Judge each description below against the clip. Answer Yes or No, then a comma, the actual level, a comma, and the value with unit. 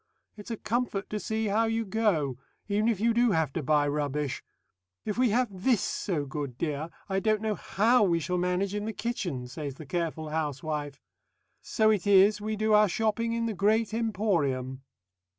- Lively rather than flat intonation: Yes, wide, 6.2 semitones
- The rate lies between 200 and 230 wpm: No, average, 185 wpm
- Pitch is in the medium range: No, high, 200 Hz